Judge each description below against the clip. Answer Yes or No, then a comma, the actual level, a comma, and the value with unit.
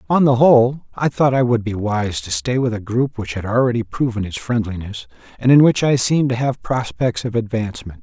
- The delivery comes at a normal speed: No, fast, 225 wpm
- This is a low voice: Yes, low, 115 Hz